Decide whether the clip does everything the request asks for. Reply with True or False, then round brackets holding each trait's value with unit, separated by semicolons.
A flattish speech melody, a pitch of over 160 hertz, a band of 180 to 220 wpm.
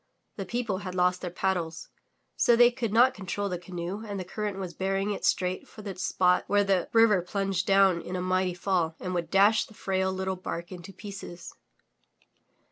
True (2.0 semitones; 190 Hz; 195 wpm)